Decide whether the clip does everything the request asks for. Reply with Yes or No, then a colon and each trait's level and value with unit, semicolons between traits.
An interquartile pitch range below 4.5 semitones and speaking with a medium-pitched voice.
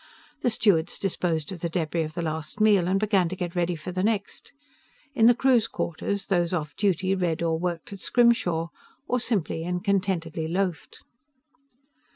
Yes: average, 3.4 semitones; medium, 180 Hz